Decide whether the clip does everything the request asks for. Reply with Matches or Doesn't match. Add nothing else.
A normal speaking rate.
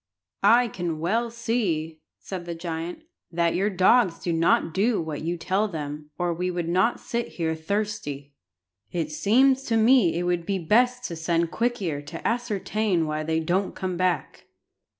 Matches